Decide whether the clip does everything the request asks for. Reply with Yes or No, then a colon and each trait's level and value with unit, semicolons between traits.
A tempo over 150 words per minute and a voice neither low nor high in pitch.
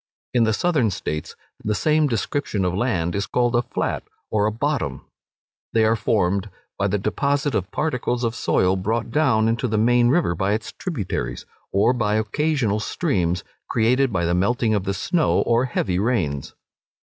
No: average, 170 wpm; low, 110 Hz